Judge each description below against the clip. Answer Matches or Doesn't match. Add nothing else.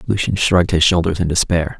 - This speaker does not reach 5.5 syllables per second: Doesn't match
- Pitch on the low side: Matches